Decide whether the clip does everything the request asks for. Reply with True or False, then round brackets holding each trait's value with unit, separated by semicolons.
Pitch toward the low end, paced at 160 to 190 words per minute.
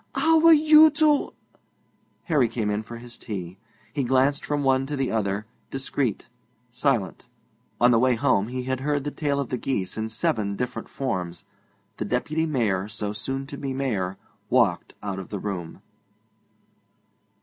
True (125 Hz; 170 wpm)